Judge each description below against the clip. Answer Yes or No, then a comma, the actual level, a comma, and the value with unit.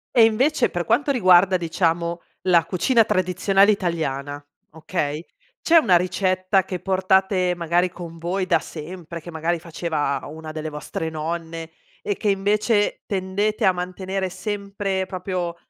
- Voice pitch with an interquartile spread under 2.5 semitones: No, average, 2.8 semitones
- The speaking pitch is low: No, medium, 180 Hz